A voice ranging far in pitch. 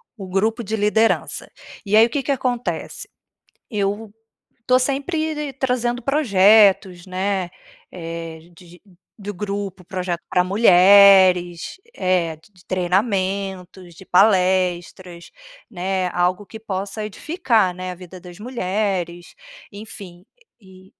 No: average, 3.2 semitones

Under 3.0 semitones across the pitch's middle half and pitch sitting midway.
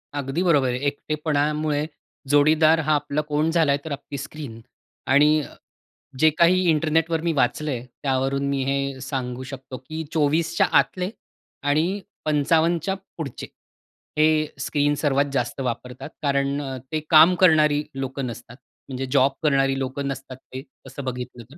Yes: narrow, 2.5 semitones; medium, 145 Hz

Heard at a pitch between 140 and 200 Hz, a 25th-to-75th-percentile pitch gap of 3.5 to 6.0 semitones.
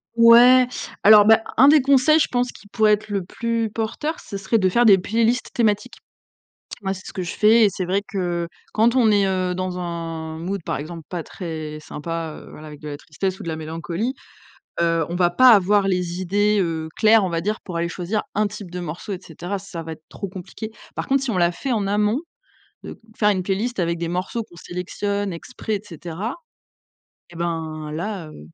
Yes: high, 190 Hz; average, 4.2 semitones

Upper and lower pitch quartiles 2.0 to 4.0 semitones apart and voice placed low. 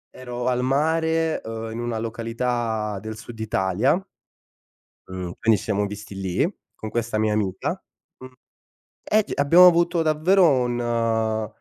No: average, 4.6 semitones; low, 115 Hz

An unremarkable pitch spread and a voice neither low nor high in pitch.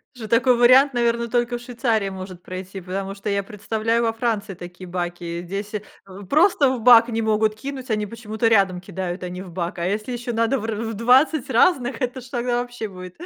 No: average, 4.1 semitones; high, 220 Hz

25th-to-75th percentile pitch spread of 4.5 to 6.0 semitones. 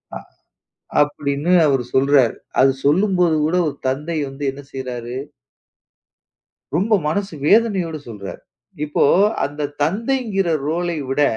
Yes: average, 4.9 semitones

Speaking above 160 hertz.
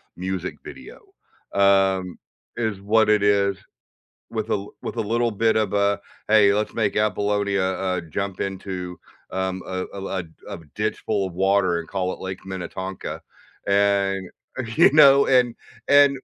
No: low, 100 Hz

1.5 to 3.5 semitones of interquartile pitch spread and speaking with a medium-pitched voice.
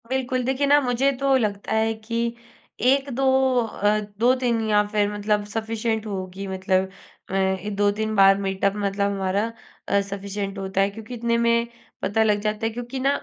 No: average, 2.8 semitones; high, 215 Hz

